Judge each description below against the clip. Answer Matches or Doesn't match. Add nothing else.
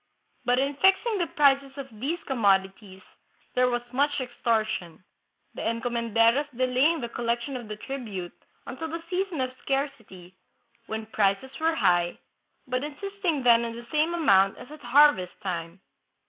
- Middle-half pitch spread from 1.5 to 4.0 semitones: Doesn't match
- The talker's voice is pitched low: Doesn't match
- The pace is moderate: Matches